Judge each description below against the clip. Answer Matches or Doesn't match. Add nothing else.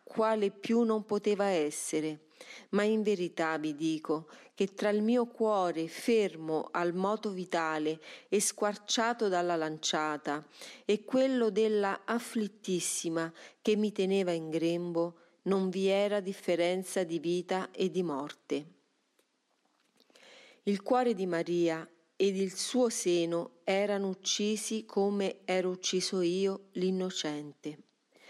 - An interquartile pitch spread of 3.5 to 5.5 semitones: Matches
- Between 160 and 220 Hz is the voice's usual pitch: Matches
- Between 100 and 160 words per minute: Matches